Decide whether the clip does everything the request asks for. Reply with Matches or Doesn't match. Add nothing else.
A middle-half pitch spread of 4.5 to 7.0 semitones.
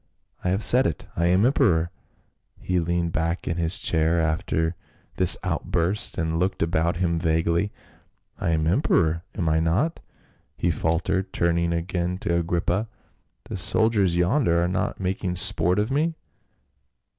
Doesn't match